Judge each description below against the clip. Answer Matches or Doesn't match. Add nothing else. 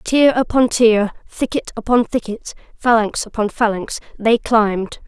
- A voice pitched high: Matches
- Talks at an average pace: Doesn't match